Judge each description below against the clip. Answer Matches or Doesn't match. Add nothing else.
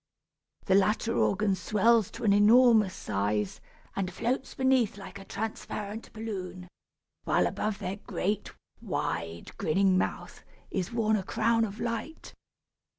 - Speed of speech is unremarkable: Doesn't match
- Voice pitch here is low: Doesn't match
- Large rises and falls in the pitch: Doesn't match